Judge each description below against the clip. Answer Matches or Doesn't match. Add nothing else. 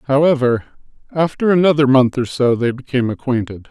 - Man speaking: Matches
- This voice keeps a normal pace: Matches